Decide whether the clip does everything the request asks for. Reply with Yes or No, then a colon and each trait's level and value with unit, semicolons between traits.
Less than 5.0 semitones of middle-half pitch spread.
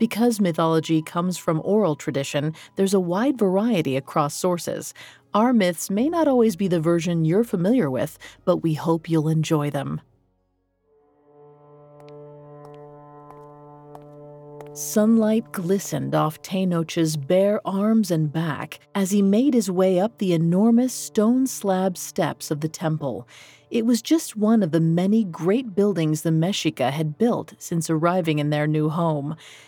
No: average, 5.3 semitones